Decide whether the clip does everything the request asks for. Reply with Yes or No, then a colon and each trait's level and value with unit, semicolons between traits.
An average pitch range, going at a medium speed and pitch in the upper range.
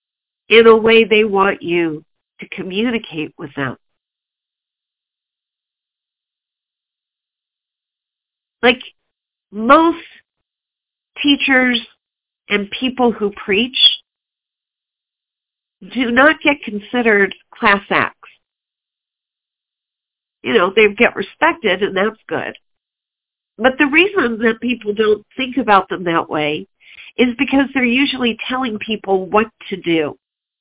No: average, 4.6 semitones; slow, 100 wpm; high, 220 Hz